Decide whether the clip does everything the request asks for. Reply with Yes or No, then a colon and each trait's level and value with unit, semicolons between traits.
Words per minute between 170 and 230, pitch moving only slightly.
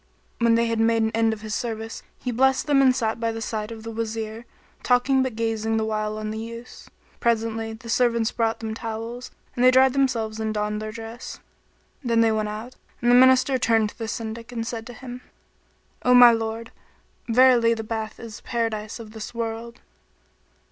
Yes: average, 200 wpm; narrow, 1.5 semitones